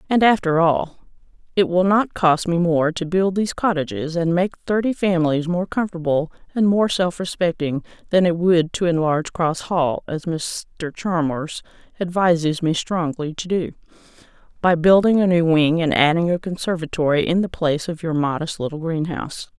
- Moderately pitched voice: Yes, medium, 170 Hz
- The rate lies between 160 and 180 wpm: Yes, average, 165 wpm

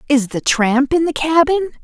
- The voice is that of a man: No, female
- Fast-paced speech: No, average, 195 wpm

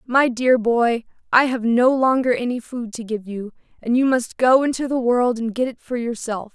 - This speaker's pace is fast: Yes, fast, 220 wpm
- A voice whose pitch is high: Yes, high, 240 Hz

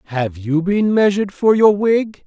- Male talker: Yes, male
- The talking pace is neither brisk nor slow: Yes, average, 185 wpm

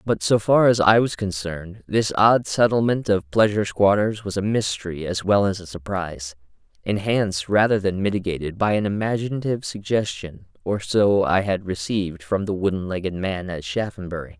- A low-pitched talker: Yes, low, 100 Hz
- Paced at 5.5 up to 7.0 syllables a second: No, 5.3 syllables/s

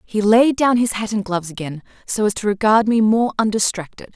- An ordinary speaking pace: No, fast, 215 wpm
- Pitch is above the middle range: Yes, high, 210 Hz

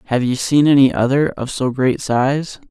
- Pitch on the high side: No, low, 135 Hz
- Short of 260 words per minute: Yes, average, 200 wpm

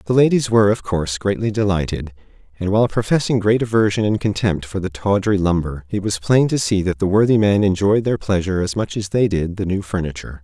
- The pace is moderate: No, fast, 220 wpm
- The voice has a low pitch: Yes, low, 100 Hz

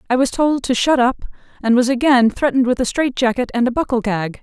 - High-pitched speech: Yes, very high, 250 Hz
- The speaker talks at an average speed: No, fast, 230 wpm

